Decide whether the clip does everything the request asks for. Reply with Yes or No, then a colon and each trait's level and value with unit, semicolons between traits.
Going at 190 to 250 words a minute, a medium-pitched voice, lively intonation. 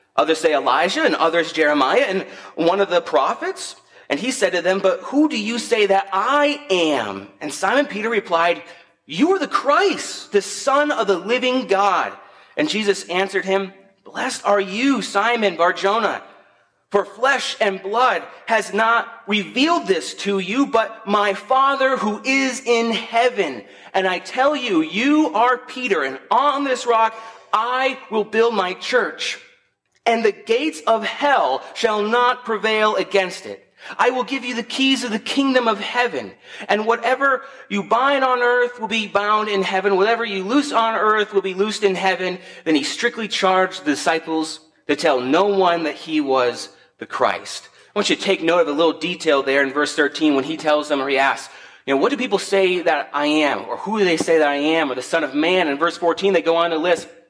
No: average, 195 wpm; high, 200 Hz; wide, 6.1 semitones